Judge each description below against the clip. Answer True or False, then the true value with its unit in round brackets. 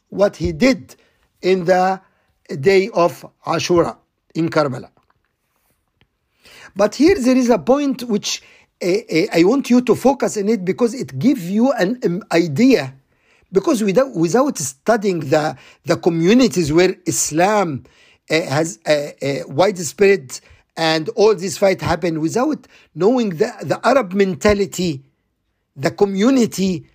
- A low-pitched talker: False (185 Hz)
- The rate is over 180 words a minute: False (135 wpm)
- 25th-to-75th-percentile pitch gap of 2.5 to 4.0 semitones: False (5.5 semitones)